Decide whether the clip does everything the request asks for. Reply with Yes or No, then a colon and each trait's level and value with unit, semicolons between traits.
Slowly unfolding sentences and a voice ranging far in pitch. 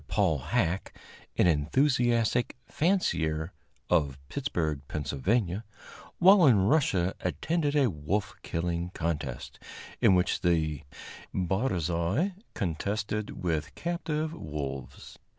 Yes: slow, 95 wpm; wide, 7.7 semitones